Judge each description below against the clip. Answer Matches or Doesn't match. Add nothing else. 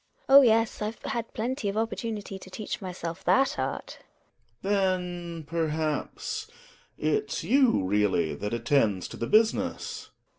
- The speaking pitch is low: Doesn't match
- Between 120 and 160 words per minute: Matches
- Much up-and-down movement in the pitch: Matches